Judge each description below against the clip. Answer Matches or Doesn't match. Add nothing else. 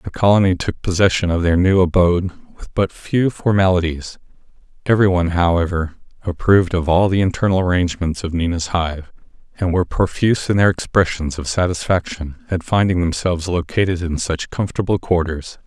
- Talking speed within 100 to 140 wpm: Doesn't match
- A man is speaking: Matches